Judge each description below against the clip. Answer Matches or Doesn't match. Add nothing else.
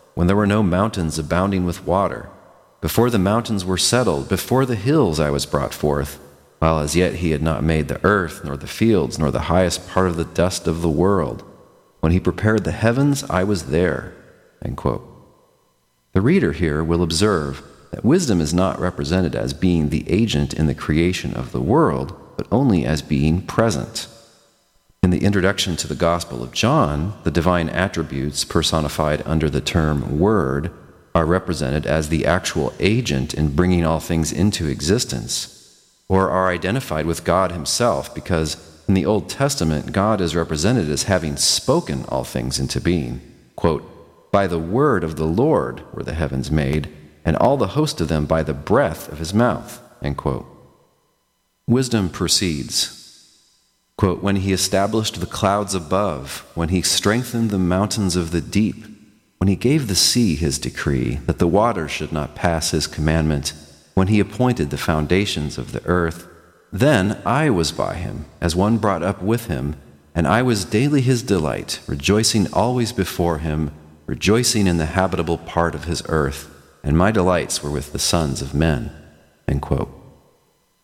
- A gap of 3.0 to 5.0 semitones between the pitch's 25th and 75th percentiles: Matches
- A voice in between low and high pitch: Doesn't match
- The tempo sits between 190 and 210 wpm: Doesn't match